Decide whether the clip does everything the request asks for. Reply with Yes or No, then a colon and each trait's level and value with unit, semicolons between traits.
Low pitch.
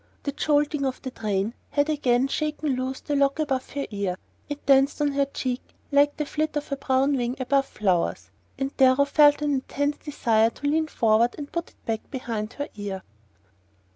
No: very high, 275 Hz